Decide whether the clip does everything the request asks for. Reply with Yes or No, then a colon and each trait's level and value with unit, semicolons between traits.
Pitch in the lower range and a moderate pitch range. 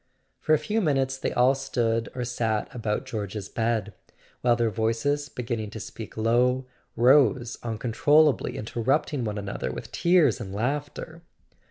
Yes: low, 120 Hz; average, 3.7 semitones